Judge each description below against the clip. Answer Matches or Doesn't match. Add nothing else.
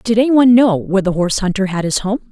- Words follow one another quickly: Matches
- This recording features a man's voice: Doesn't match